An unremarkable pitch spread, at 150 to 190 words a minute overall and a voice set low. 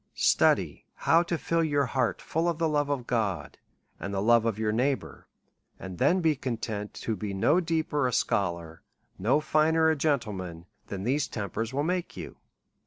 No: wide, 7.1 semitones; average, 175 wpm; low, 125 Hz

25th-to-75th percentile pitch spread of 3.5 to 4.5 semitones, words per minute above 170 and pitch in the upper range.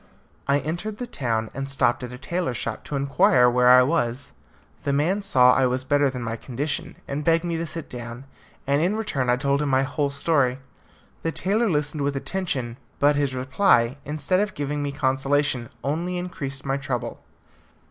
No: average, 3.9 semitones; average, 190 wpm; medium, 140 Hz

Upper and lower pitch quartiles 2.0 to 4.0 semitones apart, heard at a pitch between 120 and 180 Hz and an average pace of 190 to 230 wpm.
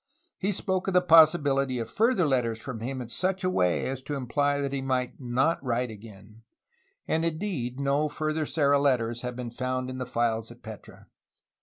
No: average, 4.4 semitones; low, 135 Hz; average, 195 wpm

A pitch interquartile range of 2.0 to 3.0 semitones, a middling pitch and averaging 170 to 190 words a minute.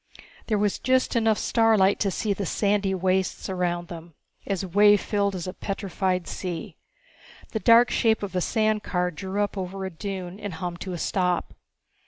No: narrow, 2.5 semitones; high, 195 Hz; average, 180 wpm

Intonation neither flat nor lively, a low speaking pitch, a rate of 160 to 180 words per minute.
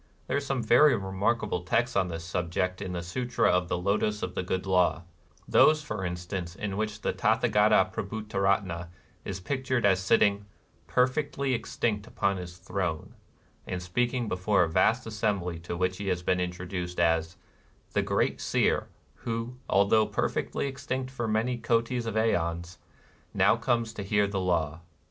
Yes: average, 4.2 semitones; low, 100 Hz; average, 165 wpm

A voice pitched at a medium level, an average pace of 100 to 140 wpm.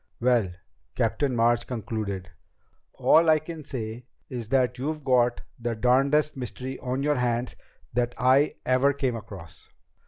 No: low, 125 Hz; slow, 135 wpm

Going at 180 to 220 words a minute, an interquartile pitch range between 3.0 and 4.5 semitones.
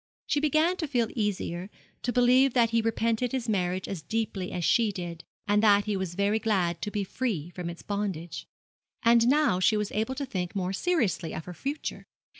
No: average, 200 wpm; average, 4.9 semitones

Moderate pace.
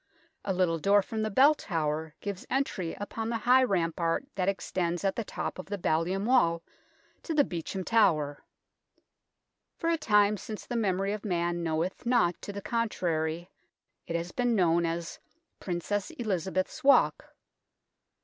Yes: average, 160 wpm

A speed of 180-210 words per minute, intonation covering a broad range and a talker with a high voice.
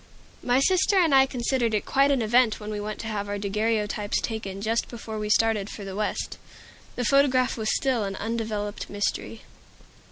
No: average, 185 wpm; average, 3.2 semitones; high, 220 Hz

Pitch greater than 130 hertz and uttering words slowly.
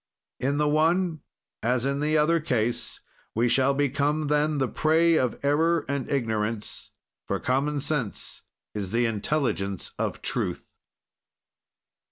Yes: medium, 140 Hz; slow, 130 wpm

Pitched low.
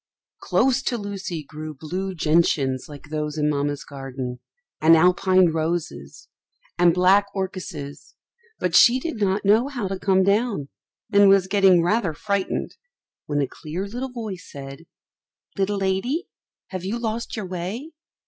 No: medium, 185 Hz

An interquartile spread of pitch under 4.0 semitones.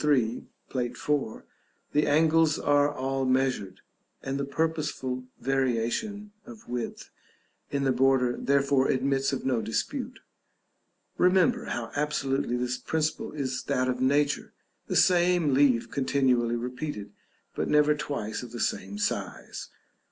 Yes: average, 3.0 semitones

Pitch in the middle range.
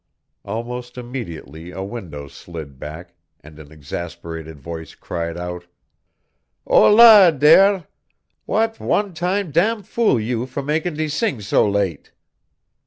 No: low, 115 Hz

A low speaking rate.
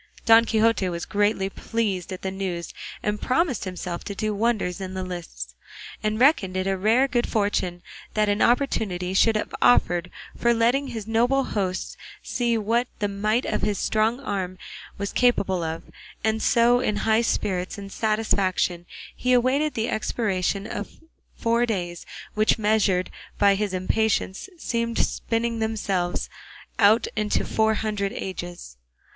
No: average, 150 wpm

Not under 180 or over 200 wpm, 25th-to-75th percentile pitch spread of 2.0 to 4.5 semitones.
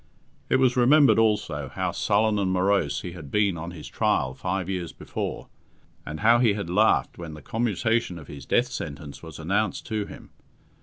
No: average, 185 wpm; average, 5.3 semitones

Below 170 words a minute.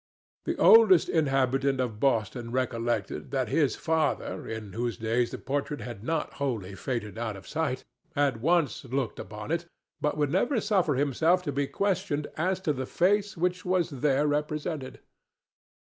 Yes: average, 150 wpm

